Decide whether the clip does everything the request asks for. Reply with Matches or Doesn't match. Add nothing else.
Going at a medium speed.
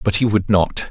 Doesn't match